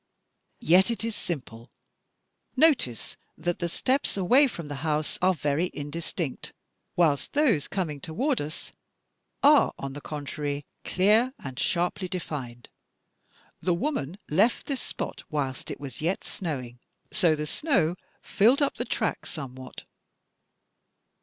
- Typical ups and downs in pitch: No, wide, 6.4 semitones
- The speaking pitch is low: No, medium, 165 Hz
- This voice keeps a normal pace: No, slow, 130 wpm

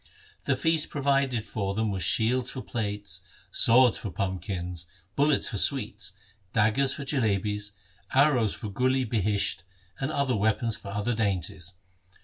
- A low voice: Yes, low, 110 Hz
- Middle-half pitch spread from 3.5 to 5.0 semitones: Yes, average, 4.5 semitones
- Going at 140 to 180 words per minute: Yes, average, 145 wpm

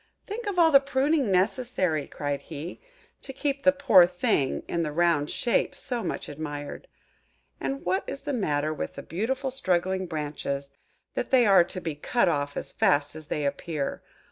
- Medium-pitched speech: Yes, medium, 180 Hz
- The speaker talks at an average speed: Yes, average, 175 wpm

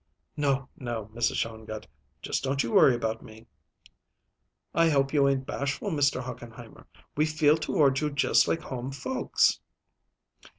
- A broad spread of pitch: No, average, 3.6 semitones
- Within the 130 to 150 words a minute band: Yes, average, 140 wpm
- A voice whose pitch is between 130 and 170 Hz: Yes, low, 135 Hz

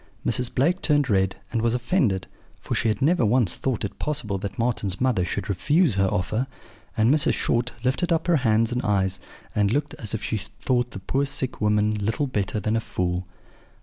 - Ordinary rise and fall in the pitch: Yes, average, 4.6 semitones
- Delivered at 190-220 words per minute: Yes, average, 200 wpm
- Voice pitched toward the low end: Yes, low, 115 Hz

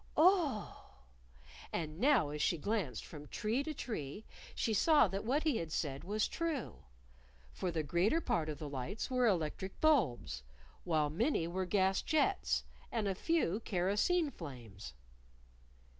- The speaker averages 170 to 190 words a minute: No, average, 145 wpm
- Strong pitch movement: Yes, wide, 8.9 semitones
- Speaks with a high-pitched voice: Yes, high, 195 Hz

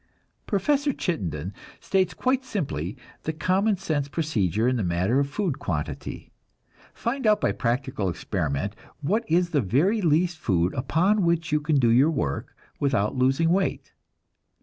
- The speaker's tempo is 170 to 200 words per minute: No, average, 150 wpm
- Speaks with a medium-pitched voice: Yes, medium, 145 Hz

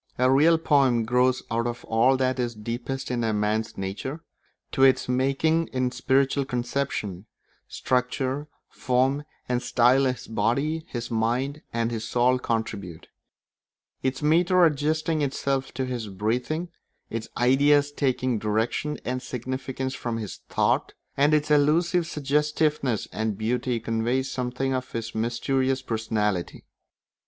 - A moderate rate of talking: No, slow, 130 wpm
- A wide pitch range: No, average, 3.2 semitones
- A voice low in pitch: Yes, low, 130 Hz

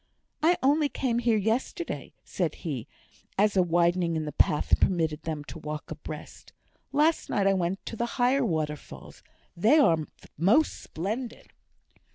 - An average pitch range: No, wide, 7.2 semitones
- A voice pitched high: Yes, high, 195 Hz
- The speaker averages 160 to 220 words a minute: No, average, 150 wpm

